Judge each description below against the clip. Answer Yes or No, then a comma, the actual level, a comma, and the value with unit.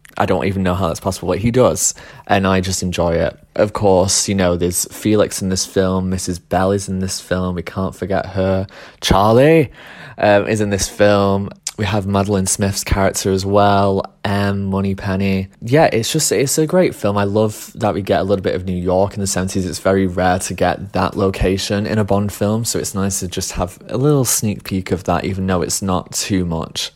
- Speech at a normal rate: No, fast, 220 wpm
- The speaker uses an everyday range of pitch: No, narrow, 1.6 semitones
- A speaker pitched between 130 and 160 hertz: No, very low, 95 Hz